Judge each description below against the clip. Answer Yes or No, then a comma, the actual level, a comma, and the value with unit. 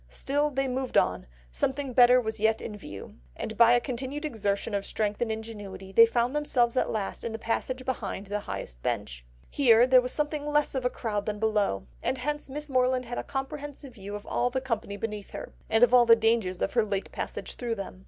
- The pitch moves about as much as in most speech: Yes, average, 3.9 semitones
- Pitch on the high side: Yes, high, 235 Hz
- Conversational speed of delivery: No, fast, 215 wpm